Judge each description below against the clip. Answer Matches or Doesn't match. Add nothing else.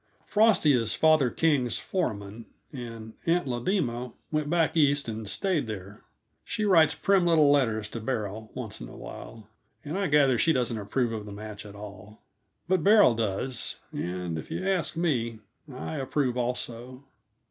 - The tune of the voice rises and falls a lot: Matches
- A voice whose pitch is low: Matches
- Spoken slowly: Doesn't match